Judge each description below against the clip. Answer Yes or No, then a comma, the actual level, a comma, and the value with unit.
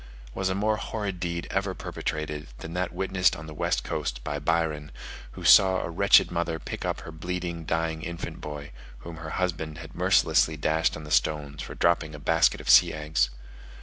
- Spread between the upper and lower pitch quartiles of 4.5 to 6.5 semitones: No, average, 2.8 semitones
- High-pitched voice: No, very low, 80 Hz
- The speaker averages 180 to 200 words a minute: Yes, average, 190 wpm